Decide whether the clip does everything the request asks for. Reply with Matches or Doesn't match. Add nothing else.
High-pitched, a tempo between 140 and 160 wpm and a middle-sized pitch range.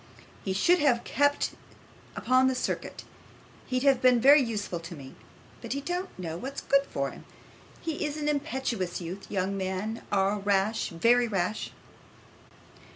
Doesn't match